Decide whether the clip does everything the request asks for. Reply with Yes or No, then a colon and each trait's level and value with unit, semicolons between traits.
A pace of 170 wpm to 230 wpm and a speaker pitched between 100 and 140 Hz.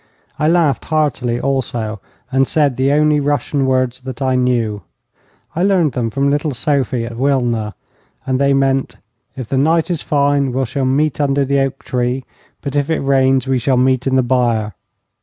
Yes: average, 180 wpm; low, 135 Hz